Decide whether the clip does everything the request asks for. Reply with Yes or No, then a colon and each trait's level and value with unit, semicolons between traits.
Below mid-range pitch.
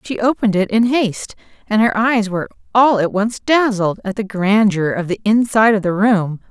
No: high, 210 Hz